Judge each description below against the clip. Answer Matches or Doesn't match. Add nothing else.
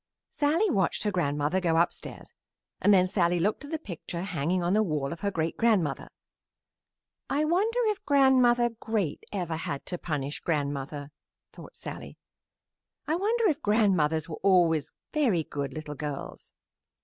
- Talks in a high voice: Doesn't match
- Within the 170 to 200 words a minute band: Doesn't match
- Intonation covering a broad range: Matches